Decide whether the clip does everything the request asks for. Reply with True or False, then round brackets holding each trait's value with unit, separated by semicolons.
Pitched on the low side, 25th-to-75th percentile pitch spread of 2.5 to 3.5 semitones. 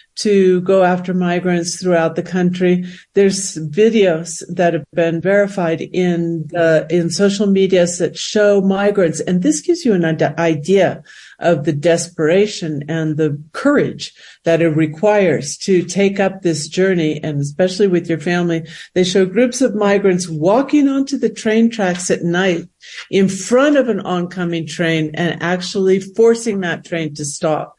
False (180 Hz; 3.1 semitones)